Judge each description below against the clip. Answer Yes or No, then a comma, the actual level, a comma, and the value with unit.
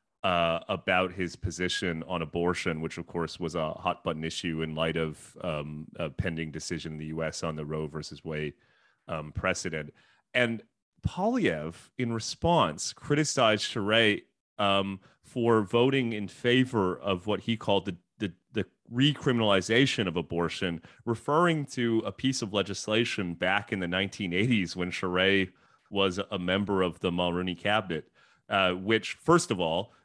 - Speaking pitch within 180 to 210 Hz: No, very low, 95 Hz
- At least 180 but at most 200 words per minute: No, average, 150 wpm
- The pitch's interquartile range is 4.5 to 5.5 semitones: Yes, average, 4.8 semitones